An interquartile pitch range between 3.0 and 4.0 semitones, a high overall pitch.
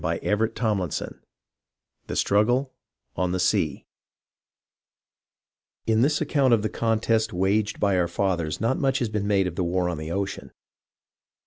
No: average, 3.7 semitones; low, 105 Hz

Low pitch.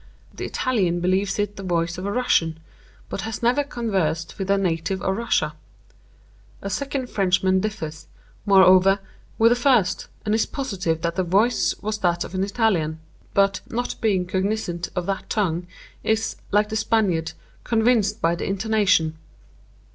No: high, 195 Hz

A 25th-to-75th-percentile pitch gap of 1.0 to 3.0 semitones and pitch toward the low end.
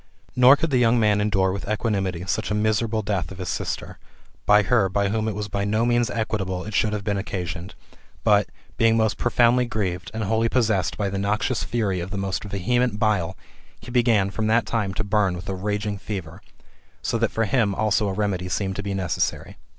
Yes: narrow, 2.5 semitones; low, 105 Hz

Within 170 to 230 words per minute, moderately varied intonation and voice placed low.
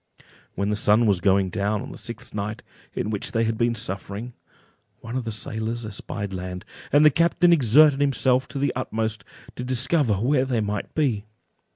Yes: average, 190 wpm; average, 4.0 semitones; low, 115 Hz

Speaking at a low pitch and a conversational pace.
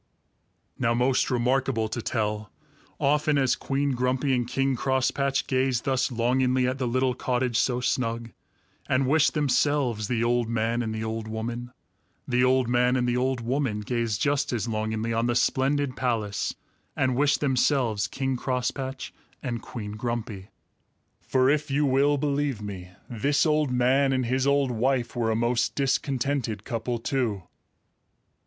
Yes: low, 125 Hz; average, 155 wpm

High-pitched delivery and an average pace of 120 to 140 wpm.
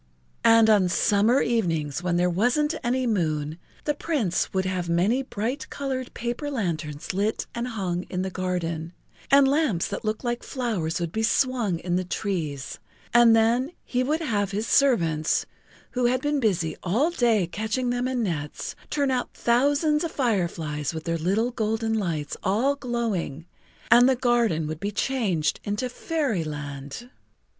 No: high, 220 Hz; average, 160 wpm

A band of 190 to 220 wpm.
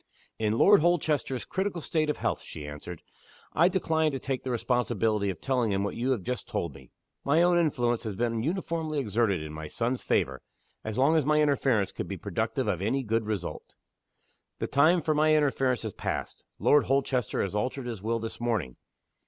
Yes: average, 195 wpm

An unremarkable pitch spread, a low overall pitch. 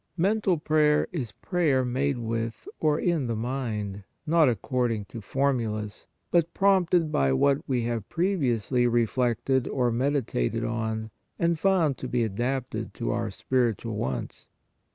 Yes: average, 5.0 semitones; low, 125 Hz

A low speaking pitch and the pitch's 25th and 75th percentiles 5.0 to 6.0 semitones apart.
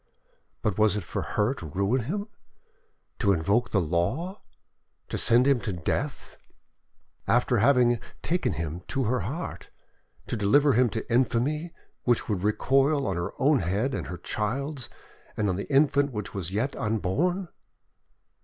Yes: low, 120 Hz; wide, 5.6 semitones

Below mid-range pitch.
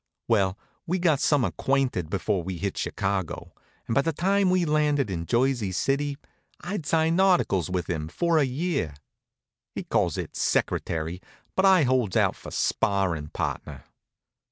Yes: low, 130 Hz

